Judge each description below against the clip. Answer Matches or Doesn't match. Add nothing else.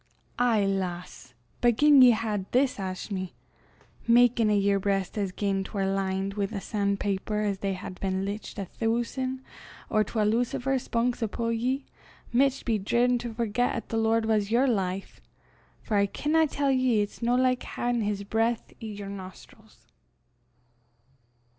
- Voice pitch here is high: Matches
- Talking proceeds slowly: Doesn't match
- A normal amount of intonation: Matches